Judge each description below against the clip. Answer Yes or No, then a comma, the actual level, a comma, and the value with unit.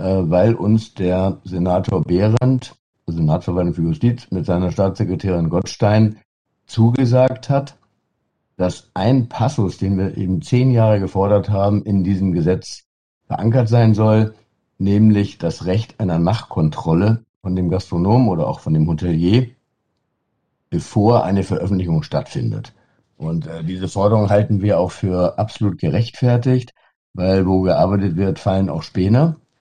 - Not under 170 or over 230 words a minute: No, average, 130 wpm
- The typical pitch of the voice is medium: No, low, 100 Hz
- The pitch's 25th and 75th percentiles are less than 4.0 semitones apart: No, average, 4.3 semitones